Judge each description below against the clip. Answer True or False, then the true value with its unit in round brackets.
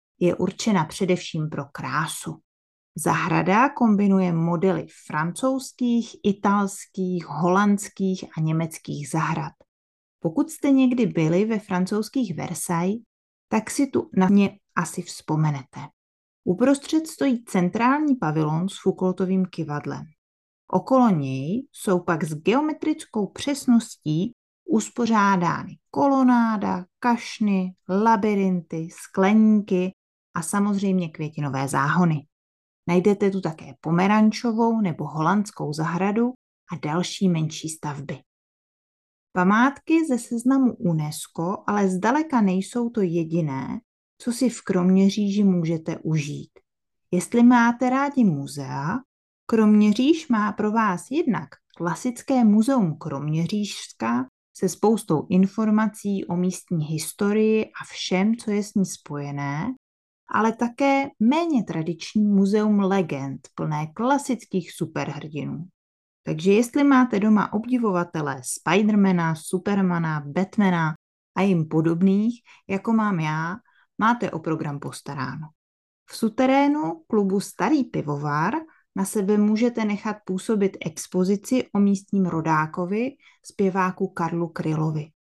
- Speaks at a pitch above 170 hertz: True (190 Hz)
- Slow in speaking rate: True (105 wpm)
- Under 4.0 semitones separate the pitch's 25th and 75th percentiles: False (5.4 semitones)